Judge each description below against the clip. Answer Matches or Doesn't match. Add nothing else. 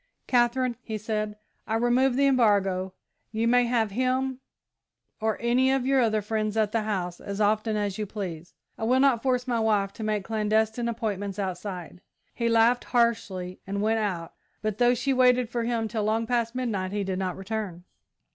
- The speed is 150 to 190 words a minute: Matches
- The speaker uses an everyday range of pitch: Matches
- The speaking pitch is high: Matches